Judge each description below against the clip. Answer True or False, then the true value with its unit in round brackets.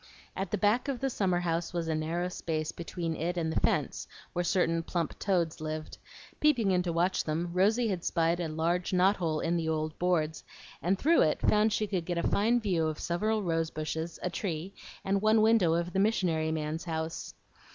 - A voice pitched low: False (175 Hz)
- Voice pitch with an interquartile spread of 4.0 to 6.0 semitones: False (3.2 semitones)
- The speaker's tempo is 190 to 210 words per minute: True (205 wpm)